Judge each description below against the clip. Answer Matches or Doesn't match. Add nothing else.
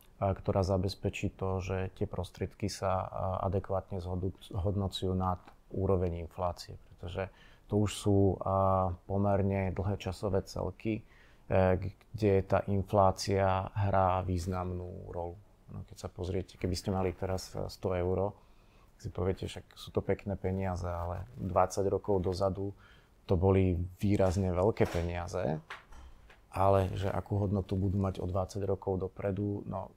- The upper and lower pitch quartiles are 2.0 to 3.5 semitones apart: Doesn't match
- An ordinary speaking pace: Matches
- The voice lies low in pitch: Matches